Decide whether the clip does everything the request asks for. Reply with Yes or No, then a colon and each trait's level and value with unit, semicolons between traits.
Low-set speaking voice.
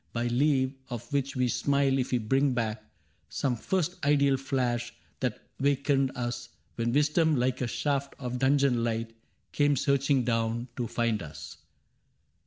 Yes: low, 130 Hz